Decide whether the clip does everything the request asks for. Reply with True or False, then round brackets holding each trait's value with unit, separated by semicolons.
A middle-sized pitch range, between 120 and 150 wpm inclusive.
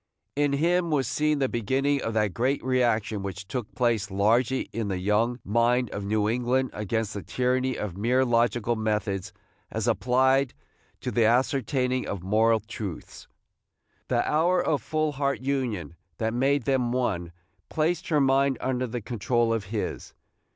False (3.6 semitones; 160 wpm)